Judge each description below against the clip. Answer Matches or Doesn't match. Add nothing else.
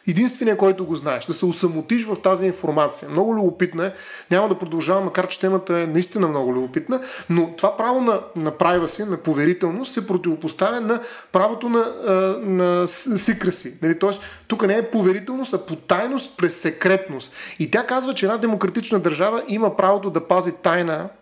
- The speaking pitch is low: Doesn't match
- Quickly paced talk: Matches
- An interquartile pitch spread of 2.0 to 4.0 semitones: Matches